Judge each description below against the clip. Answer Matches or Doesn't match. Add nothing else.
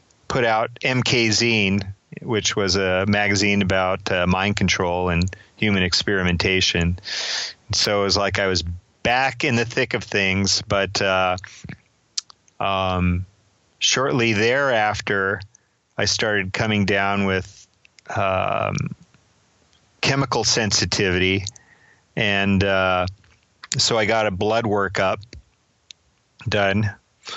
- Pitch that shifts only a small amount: Matches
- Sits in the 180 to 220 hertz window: Doesn't match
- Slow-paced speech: Matches